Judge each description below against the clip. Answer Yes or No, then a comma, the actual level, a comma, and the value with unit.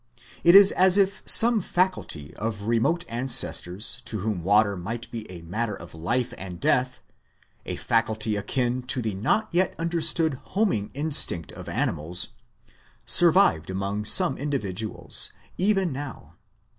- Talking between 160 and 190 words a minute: No, slow, 135 wpm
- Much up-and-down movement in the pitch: Yes, wide, 8.7 semitones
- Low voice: Yes, low, 120 Hz